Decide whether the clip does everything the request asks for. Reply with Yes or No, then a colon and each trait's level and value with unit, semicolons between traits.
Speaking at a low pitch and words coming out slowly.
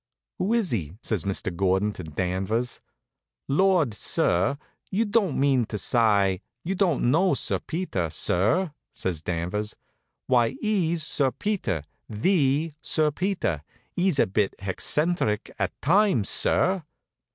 Yes: low, 125 Hz; slow, 130 wpm